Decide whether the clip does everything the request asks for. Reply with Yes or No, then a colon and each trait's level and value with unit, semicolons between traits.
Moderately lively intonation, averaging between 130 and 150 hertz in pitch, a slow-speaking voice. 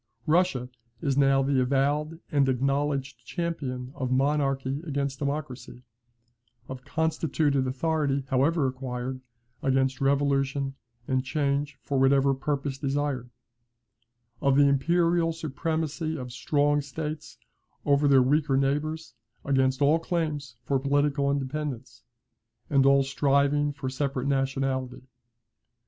No: narrow, 1.8 semitones; medium, 140 Hz; slow, 110 wpm